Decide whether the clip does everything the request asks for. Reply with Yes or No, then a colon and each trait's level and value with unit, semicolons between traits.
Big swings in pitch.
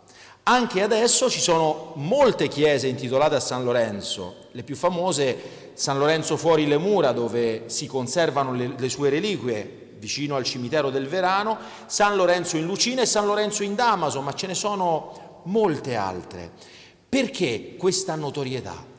Yes: wide, 6.4 semitones